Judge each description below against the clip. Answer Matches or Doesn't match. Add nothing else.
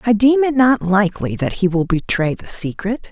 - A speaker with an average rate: Doesn't match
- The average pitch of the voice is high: Matches